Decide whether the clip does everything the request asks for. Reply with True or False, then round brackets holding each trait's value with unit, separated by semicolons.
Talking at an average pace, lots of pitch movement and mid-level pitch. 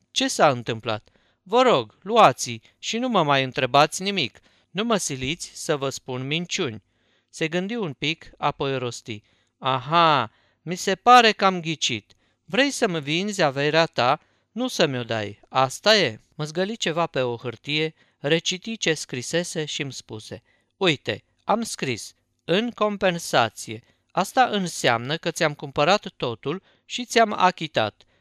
True (145 wpm; 7.4 semitones; 155 Hz)